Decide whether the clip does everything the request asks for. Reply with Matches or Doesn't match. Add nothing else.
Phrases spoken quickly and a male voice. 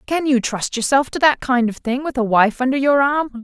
Doesn't match